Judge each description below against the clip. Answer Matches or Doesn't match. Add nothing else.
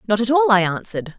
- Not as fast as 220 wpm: Doesn't match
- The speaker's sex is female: Matches